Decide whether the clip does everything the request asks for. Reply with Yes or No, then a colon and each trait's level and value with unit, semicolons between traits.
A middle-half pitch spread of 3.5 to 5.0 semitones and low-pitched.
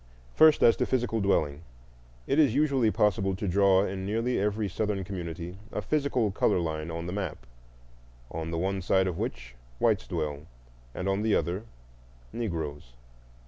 Yes: average, 4.6 semitones; very low, 95 Hz